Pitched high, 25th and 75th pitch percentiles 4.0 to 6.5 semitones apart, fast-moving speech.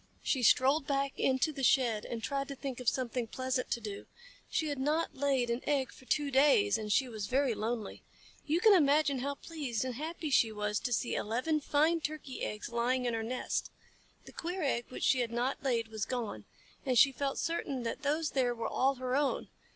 No: very high, 260 Hz; average, 3.3 semitones; fast, 210 wpm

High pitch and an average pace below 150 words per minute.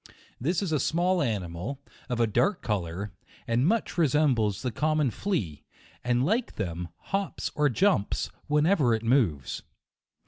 No: low, 130 Hz; average, 140 wpm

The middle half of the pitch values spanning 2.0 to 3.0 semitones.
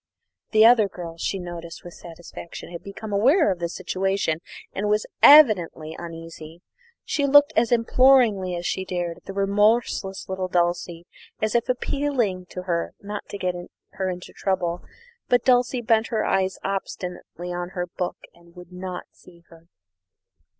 No: average, 3.8 semitones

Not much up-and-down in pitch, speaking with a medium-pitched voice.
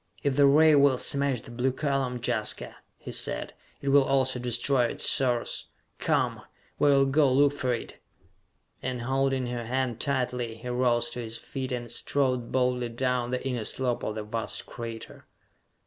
No: narrow, 2.2 semitones; low, 125 Hz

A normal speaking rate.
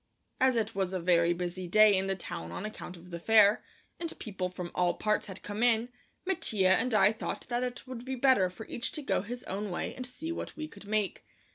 No: fast, 235 wpm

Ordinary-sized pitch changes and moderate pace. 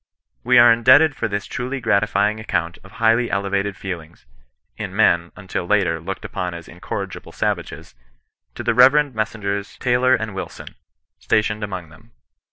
Yes: average, 3.7 semitones; average, 150 wpm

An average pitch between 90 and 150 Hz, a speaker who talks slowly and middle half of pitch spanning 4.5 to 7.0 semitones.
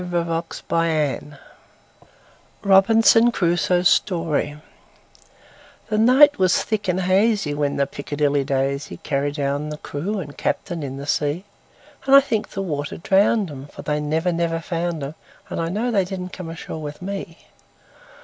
No: medium, 165 Hz; slow, 130 wpm; average, 4.8 semitones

